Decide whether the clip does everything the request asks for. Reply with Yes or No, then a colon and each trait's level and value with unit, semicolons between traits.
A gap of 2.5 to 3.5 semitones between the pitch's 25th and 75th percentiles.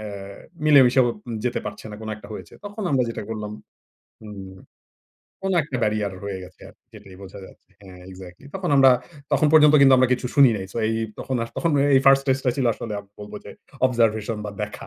No: average, 4.6 semitones